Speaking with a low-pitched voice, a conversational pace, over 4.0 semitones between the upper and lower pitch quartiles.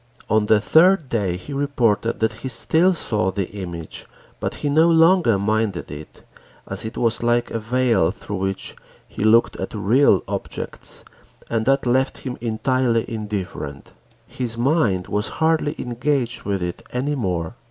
Yes: low, 115 Hz; average, 155 wpm; average, 4.7 semitones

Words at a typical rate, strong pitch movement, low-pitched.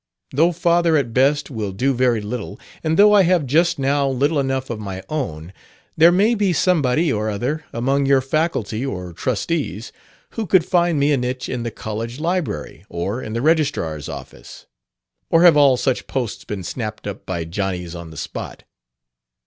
Yes: average, 180 wpm; wide, 6.8 semitones; low, 130 Hz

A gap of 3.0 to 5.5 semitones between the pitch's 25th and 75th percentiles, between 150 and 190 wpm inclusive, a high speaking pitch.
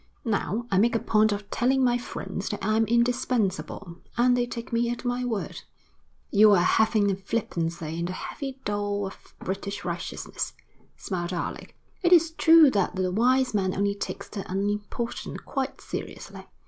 Yes: average, 3.8 semitones; average, 170 wpm; high, 210 Hz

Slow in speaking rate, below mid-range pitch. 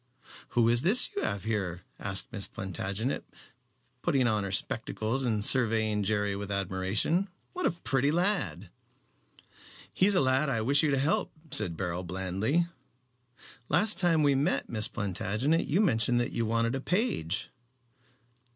No: average, 150 wpm; low, 115 Hz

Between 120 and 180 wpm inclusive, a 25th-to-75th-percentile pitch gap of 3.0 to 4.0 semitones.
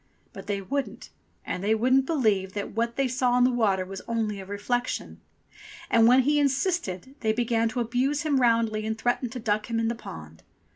No: average, 200 wpm; average, 3.3 semitones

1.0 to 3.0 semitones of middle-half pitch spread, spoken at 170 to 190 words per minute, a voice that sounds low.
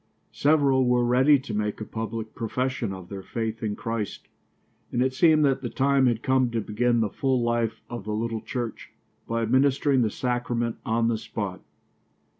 Yes: average, 2.7 semitones; average, 180 wpm; low, 120 Hz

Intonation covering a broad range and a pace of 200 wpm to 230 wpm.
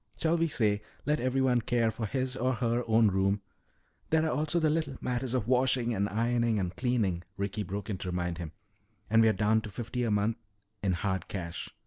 No: average, 4.0 semitones; fast, 205 wpm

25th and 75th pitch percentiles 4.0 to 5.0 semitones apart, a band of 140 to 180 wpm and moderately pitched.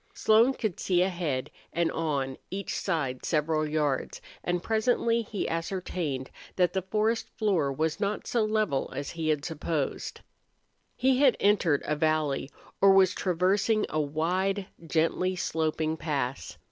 Yes: average, 4.6 semitones; average, 145 wpm; medium, 170 Hz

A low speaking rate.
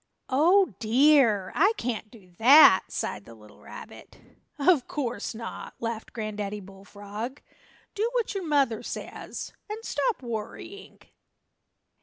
Yes: slow, 120 wpm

